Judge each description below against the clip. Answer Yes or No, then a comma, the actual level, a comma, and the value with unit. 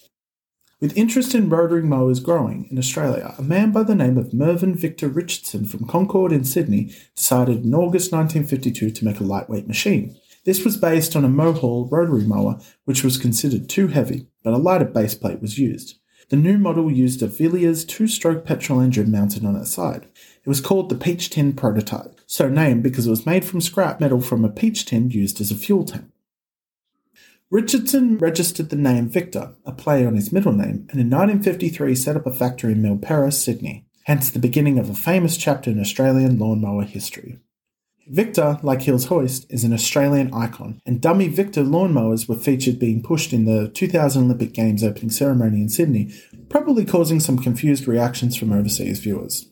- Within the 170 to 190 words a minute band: Yes, average, 185 wpm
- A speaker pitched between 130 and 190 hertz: Yes, low, 135 Hz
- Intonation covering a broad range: Yes, wide, 6.5 semitones